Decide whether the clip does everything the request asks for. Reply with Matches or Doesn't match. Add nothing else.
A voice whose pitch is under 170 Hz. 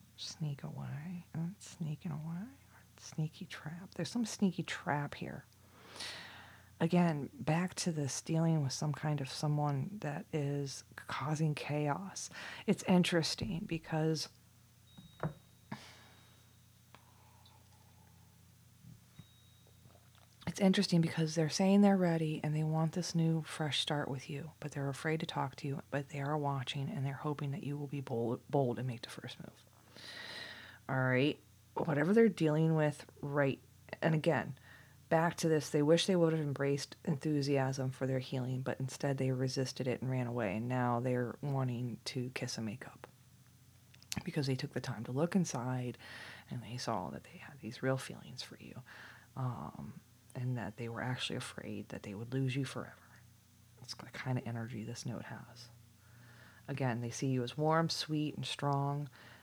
Matches